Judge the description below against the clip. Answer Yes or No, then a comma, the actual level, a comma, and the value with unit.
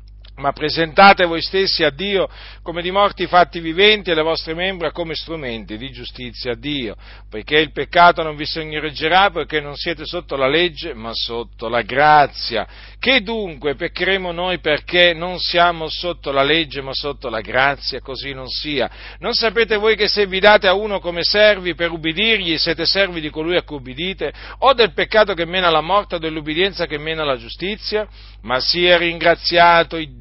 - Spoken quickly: Yes, fast, 180 wpm